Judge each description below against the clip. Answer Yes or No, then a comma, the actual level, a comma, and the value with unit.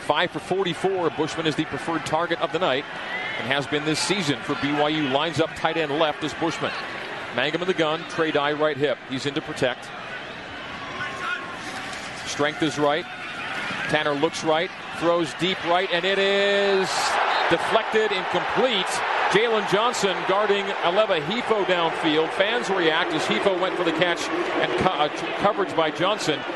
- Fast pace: No, average, 160 wpm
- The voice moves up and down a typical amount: Yes, average, 3.5 semitones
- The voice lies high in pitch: No, medium, 160 Hz